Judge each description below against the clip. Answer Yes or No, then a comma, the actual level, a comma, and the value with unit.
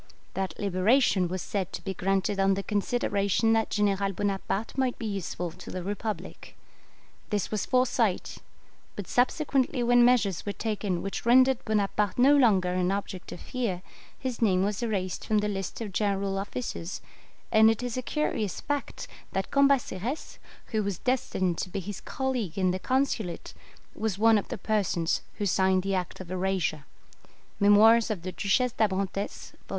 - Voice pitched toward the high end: Yes, high, 205 Hz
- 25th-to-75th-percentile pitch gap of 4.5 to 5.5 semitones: No, average, 3.5 semitones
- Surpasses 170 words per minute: No, average, 165 wpm